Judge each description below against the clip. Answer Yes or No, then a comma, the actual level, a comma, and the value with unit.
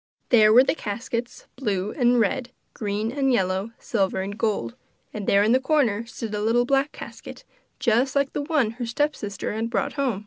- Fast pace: No, average, 185 wpm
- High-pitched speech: Yes, high, 230 Hz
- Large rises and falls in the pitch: No, average, 4.1 semitones